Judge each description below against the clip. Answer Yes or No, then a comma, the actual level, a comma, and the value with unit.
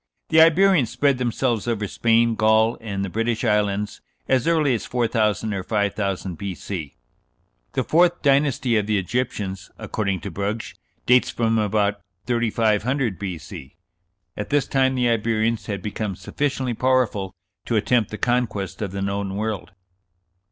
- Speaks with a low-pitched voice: Yes, low, 110 Hz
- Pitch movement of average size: Yes, average, 3.7 semitones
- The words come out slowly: No, average, 145 wpm